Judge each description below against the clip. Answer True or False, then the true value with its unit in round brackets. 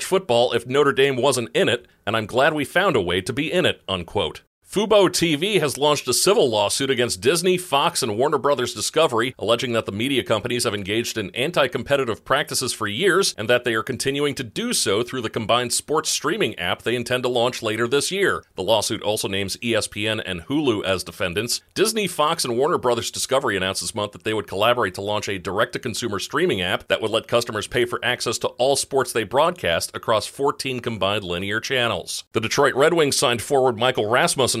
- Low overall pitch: True (120 Hz)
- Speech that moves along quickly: True (210 wpm)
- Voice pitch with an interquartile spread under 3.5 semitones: False (4.7 semitones)